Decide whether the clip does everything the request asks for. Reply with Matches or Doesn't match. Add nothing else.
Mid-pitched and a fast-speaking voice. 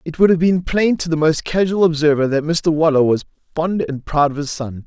Matches